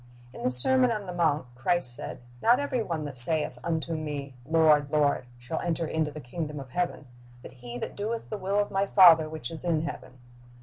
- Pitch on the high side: No, medium, 155 Hz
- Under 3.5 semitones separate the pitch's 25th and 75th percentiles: No, average, 4.2 semitones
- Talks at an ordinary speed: No, fast, 215 wpm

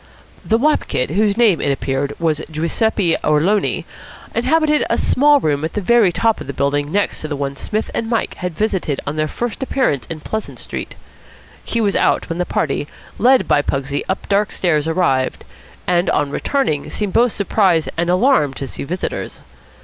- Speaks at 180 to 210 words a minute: Yes, average, 185 wpm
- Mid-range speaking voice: Yes, medium, 180 Hz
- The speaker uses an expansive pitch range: Yes, wide, 6.9 semitones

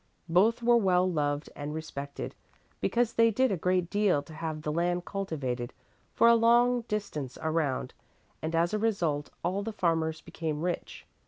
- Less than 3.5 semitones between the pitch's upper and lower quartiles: No, wide, 5.5 semitones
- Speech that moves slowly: No, average, 165 wpm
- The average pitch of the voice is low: No, medium, 175 Hz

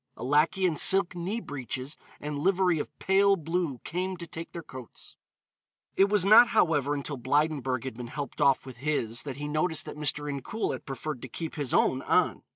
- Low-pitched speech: No, medium, 150 Hz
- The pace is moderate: Yes, average, 195 wpm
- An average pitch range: Yes, average, 4.7 semitones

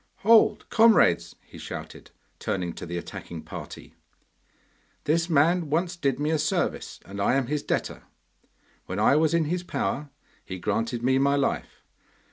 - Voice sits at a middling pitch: Yes, medium, 145 Hz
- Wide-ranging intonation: Yes, wide, 6.5 semitones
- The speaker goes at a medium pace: Yes, average, 155 wpm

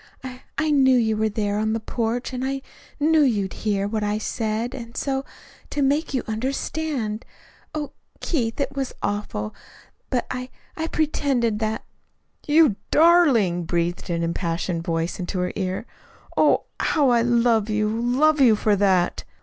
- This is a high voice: Yes, high, 230 Hz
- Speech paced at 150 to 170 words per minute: Yes, average, 165 wpm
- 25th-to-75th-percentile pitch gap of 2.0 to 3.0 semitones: No, average, 4.8 semitones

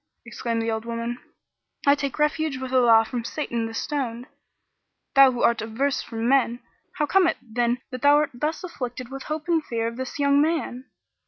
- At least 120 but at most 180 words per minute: No, average, 190 wpm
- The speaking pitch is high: Yes, very high, 255 Hz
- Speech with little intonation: No, average, 3.8 semitones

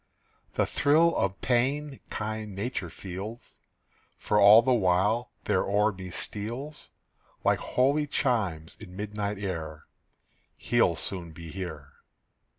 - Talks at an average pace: No, slow, 120 wpm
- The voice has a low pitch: Yes, low, 105 Hz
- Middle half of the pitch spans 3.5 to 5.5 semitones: Yes, average, 4.6 semitones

